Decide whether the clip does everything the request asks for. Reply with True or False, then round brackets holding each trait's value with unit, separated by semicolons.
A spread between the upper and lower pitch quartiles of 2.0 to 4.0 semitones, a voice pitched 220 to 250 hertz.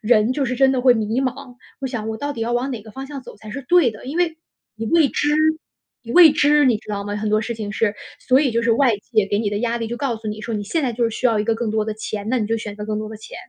True (3.5 semitones; 230 Hz)